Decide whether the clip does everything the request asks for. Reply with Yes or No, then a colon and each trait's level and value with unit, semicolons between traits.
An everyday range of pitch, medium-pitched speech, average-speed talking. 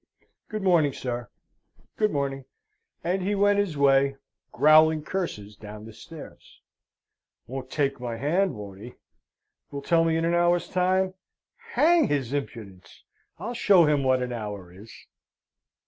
No: wide, 6.6 semitones; medium, 145 Hz; average, 145 wpm